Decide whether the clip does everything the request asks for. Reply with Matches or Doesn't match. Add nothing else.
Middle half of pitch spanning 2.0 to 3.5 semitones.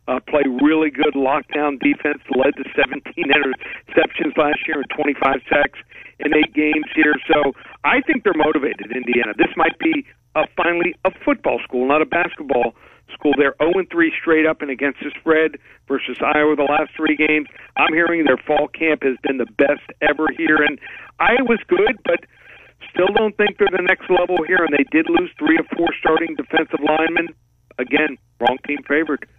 Matches